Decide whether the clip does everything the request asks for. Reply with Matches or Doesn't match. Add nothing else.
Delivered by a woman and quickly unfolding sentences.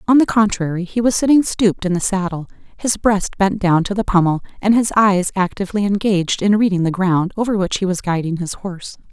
Matches